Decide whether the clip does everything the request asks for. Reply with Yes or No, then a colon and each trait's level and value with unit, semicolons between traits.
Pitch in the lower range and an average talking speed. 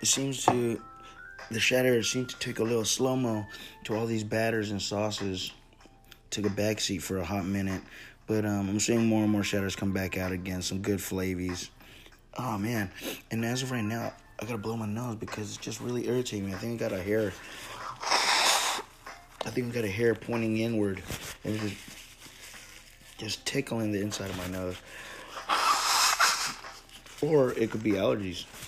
Yes: low, 110 Hz; average, 180 wpm